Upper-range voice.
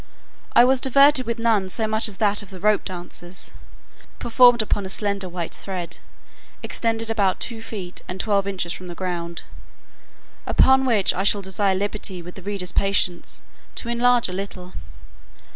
Yes: high, 200 Hz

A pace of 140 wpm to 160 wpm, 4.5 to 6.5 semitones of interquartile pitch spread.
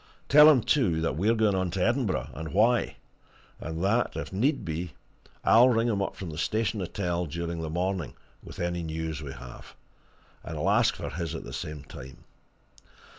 No: average, 185 wpm; average, 5.3 semitones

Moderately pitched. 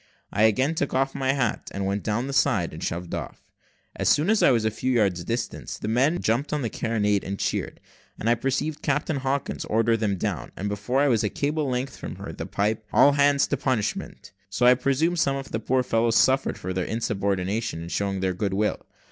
No: low, 115 Hz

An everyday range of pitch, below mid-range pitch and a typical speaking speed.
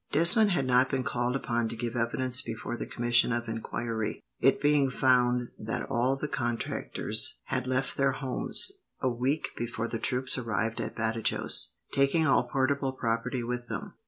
No: narrow, 2.3 semitones; low, 125 Hz; average, 165 wpm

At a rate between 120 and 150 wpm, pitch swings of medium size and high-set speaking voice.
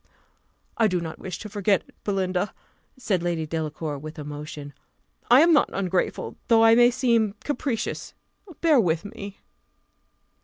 No: average, 145 wpm; wide, 6.0 semitones; high, 195 Hz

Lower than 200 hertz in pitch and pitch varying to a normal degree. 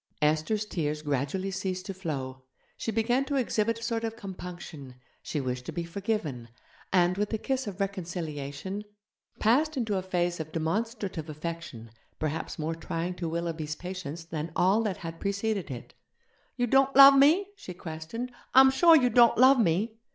No: medium, 185 Hz; wide, 6.0 semitones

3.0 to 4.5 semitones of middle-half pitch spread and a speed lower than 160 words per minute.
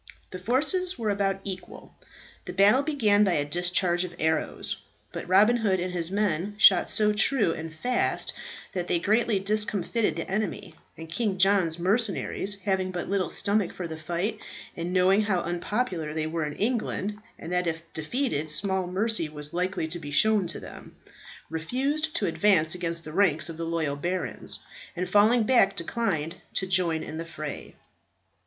No: average, 4.0 semitones; average, 170 wpm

